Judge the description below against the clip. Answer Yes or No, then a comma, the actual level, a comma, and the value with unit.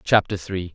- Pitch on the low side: Yes, very low, 90 Hz